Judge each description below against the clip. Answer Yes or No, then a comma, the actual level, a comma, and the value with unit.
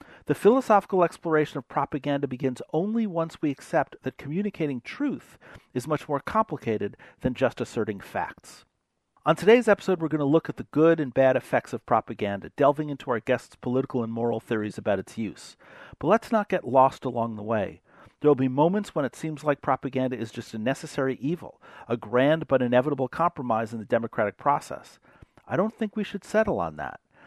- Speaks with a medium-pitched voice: Yes, medium, 145 Hz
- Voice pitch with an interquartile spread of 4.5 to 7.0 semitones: Yes, average, 4.9 semitones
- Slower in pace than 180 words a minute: No, average, 190 wpm